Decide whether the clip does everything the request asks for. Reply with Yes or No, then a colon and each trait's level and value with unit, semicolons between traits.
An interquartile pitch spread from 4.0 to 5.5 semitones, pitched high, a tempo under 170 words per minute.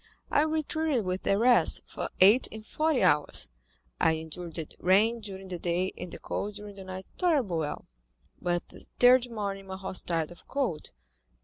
No: average, 5.2 semitones; high, 195 Hz; average, 180 wpm